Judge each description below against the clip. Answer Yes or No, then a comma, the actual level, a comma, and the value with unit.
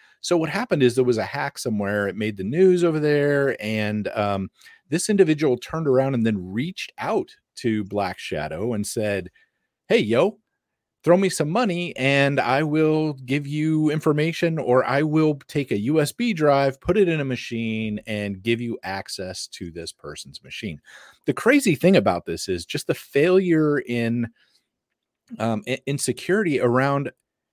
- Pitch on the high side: No, low, 135 Hz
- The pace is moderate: Yes, average, 165 wpm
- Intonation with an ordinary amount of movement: No, wide, 5.9 semitones